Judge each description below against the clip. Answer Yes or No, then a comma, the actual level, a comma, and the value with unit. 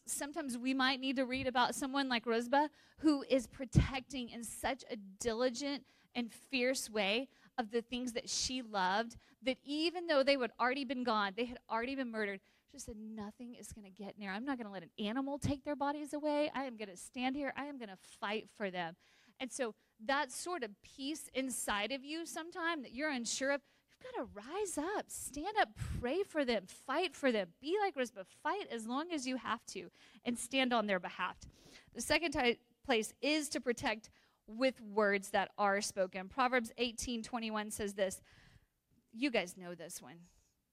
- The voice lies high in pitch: Yes, very high, 250 Hz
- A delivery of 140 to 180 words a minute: No, average, 200 wpm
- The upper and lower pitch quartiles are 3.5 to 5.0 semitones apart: Yes, average, 4.4 semitones